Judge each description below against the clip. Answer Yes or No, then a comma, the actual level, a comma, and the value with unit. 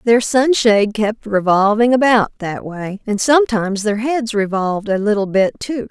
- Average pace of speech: Yes, average, 165 wpm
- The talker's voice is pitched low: No, high, 220 Hz